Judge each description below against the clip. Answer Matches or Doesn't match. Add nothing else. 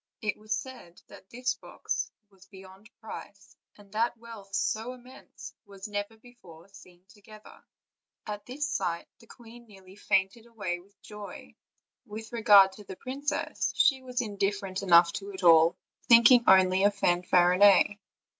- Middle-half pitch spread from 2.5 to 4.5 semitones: Matches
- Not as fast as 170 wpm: Matches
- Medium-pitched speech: Doesn't match